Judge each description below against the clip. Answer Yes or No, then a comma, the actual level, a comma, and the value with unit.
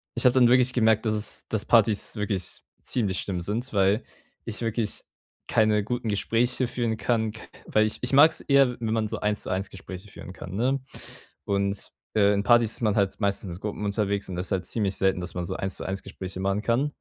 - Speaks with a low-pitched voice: Yes, low, 105 Hz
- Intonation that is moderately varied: Yes, average, 3.0 semitones